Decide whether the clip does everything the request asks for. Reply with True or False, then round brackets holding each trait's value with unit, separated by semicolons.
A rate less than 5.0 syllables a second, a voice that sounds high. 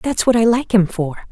False (5.3 syllables/s; 210 Hz)